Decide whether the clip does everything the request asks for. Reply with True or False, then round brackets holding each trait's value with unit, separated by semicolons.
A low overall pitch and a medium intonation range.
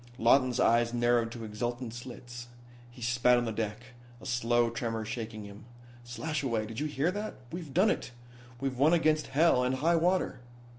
True (120 Hz; 3.4 semitones)